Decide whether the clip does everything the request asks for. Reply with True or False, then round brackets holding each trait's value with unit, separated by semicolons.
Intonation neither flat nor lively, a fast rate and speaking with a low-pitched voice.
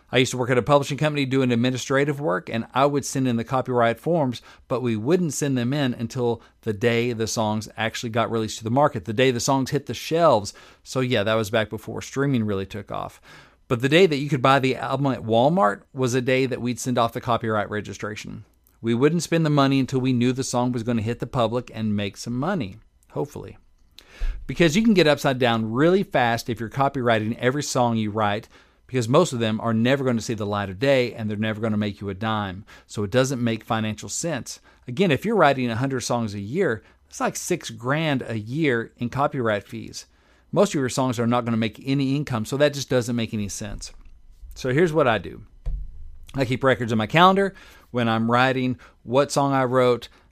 True (3.6 semitones; 230 wpm; 120 Hz)